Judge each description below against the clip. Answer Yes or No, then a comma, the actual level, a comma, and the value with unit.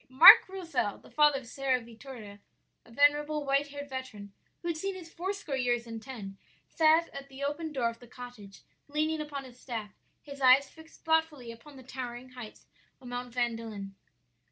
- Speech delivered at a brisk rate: No, average, 180 wpm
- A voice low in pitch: No, very high, 265 Hz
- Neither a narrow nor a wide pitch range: Yes, average, 4.0 semitones